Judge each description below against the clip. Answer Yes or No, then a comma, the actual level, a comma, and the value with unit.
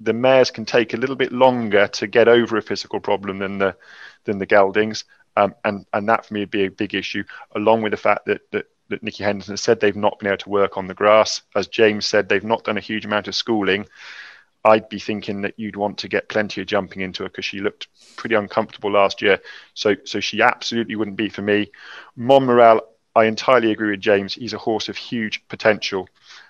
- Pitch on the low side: Yes, low, 105 Hz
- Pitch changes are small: Yes, narrow, 1.9 semitones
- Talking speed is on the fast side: Yes, fast, 225 wpm